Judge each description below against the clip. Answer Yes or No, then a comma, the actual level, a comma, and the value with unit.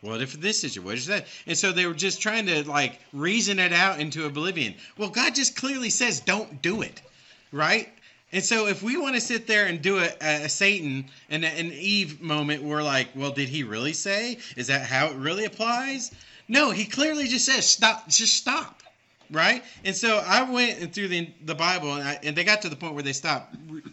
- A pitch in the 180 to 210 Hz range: Yes, medium, 185 Hz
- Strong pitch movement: Yes, wide, 6.5 semitones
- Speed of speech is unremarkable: No, fast, 220 wpm